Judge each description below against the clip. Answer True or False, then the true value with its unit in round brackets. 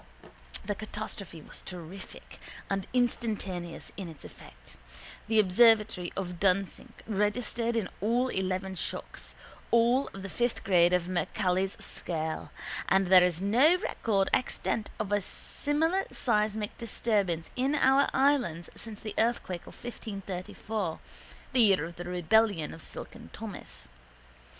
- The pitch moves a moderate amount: True (4.2 semitones)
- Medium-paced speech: False (130 wpm)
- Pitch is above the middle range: True (200 Hz)